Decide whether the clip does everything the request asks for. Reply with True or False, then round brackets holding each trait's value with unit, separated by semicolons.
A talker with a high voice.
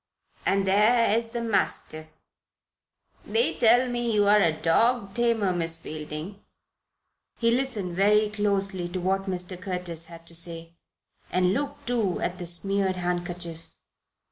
True (195 Hz)